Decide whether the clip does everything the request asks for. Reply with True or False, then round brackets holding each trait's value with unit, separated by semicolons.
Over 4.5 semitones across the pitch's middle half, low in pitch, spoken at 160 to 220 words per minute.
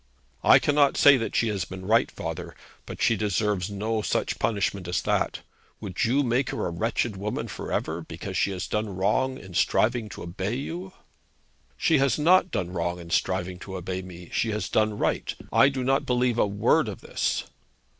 True (4.9 semitones; 105 Hz; 195 wpm)